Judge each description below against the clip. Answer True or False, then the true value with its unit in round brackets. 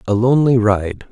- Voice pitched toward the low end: True (115 Hz)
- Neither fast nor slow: True (160 wpm)